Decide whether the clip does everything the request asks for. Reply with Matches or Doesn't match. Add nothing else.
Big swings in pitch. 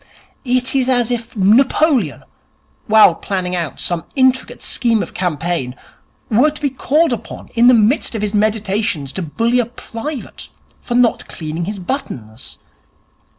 Matches